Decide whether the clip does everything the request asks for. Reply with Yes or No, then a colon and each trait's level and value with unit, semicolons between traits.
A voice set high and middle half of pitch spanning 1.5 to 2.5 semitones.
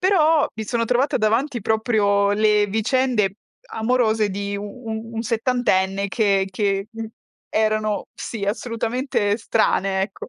No: high, 220 Hz; average, 2.9 semitones